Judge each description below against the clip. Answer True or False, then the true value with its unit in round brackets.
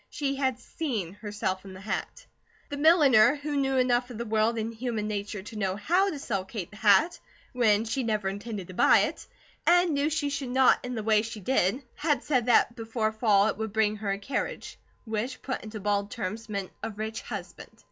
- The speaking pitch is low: False (225 Hz)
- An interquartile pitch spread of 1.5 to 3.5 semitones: False (4.1 semitones)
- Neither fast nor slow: False (210 wpm)